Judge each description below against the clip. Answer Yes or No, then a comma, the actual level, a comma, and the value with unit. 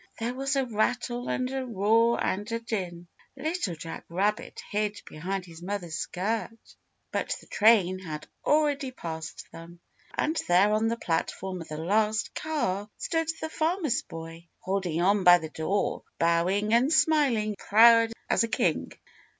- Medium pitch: No, high, 210 Hz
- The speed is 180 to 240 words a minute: No, average, 160 wpm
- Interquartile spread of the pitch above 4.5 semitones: Yes, average, 5.2 semitones